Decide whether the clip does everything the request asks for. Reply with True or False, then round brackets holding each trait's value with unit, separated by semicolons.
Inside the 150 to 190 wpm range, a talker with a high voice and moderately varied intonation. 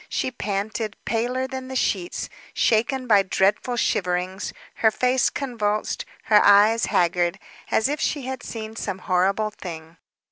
False (140 wpm; 215 Hz; 4.5 semitones)